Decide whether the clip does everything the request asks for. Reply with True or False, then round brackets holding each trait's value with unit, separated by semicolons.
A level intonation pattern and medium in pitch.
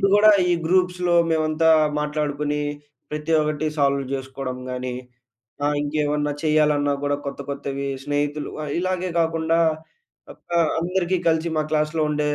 True (2.1 semitones; 150 Hz)